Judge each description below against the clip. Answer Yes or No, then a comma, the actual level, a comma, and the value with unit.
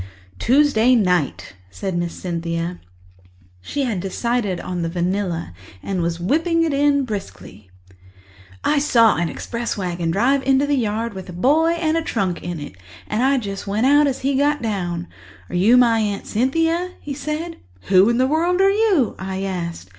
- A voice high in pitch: Yes, high, 225 Hz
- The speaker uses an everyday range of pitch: No, wide, 8.1 semitones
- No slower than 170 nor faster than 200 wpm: Yes, average, 175 wpm